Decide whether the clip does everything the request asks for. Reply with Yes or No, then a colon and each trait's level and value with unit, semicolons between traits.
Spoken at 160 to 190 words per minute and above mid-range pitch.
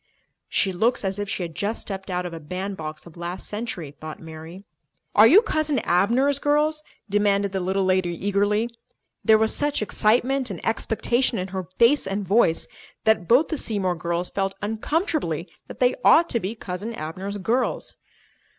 Yes: average, 170 wpm; high, 200 Hz